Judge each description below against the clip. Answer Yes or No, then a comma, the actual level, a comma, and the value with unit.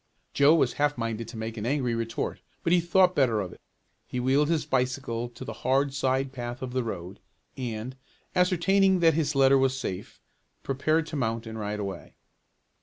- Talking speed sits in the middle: Yes, average, 185 wpm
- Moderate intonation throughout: Yes, average, 4.3 semitones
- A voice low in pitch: Yes, low, 130 Hz